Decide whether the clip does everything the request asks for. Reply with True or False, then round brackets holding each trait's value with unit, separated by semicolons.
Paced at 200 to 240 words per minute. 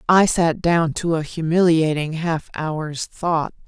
False (145 wpm)